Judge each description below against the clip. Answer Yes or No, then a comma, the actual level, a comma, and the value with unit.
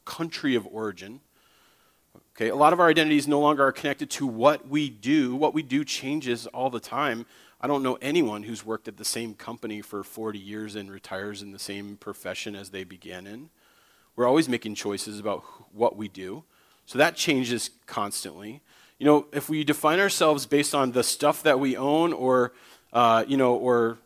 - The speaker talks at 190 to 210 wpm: Yes, average, 195 wpm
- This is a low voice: Yes, low, 120 Hz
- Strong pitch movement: Yes, wide, 5.7 semitones